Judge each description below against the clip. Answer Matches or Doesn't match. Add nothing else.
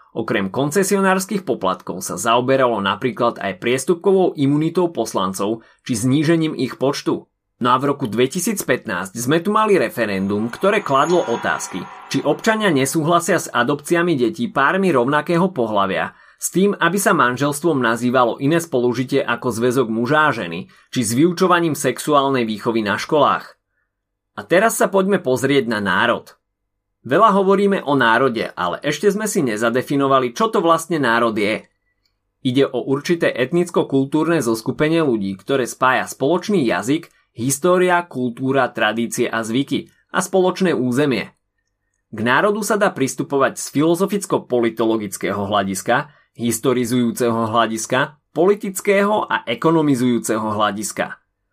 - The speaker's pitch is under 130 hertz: Doesn't match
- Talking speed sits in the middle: Matches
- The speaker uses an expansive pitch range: Matches